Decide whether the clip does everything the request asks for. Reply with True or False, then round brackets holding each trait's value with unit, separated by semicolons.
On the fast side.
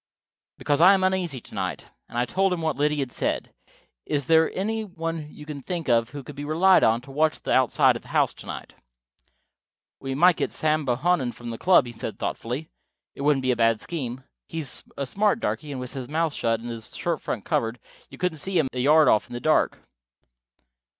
True (220 wpm)